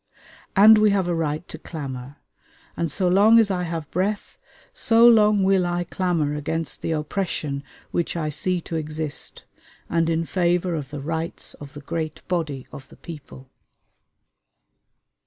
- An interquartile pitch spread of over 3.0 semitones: Yes, average, 3.6 semitones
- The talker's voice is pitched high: No, medium, 165 Hz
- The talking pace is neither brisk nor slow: Yes, average, 155 wpm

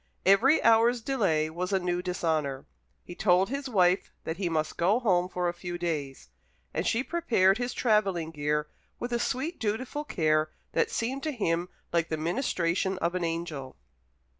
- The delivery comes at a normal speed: Yes, average, 170 wpm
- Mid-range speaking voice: Yes, medium, 180 Hz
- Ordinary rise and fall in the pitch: No, wide, 5.7 semitones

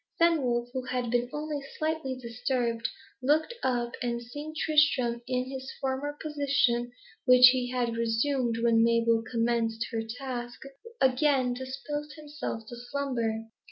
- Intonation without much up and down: No, average, 3.1 semitones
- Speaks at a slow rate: Yes, slow, 130 wpm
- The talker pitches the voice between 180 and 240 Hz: No, very high, 250 Hz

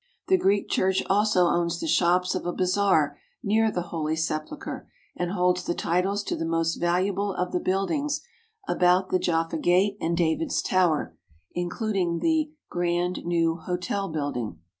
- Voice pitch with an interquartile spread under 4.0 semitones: Yes, average, 2.7 semitones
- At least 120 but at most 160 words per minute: Yes, average, 155 wpm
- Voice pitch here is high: No, medium, 180 Hz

